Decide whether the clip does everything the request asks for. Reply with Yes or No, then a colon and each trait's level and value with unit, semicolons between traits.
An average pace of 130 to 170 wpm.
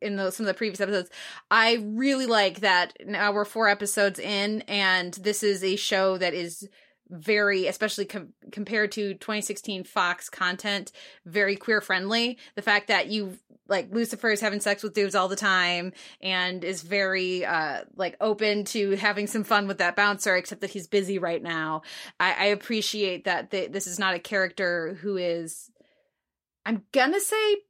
No: average, 180 wpm